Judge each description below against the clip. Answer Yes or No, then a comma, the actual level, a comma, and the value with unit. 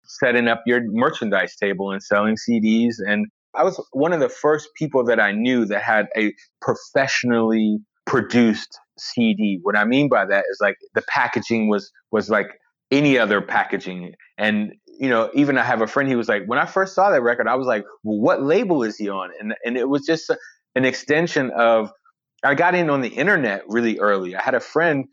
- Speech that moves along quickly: Yes, fast, 210 wpm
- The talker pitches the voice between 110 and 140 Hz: Yes, low, 115 Hz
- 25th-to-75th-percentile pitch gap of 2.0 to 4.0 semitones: No, average, 4.8 semitones